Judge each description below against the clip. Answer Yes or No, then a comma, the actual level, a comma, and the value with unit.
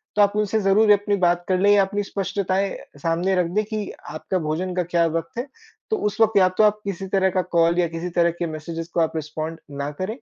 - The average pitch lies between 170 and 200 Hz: Yes, medium, 185 Hz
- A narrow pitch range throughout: No, average, 3.3 semitones